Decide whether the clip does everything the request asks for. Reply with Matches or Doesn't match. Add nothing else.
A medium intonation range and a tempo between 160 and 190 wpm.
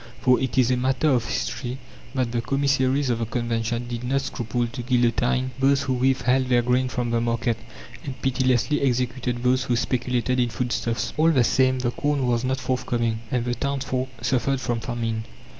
Doesn't match